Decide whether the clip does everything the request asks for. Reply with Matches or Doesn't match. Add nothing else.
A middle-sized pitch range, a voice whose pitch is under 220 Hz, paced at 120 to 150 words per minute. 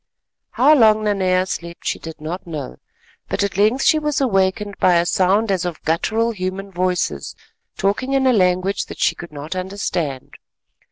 Doesn't match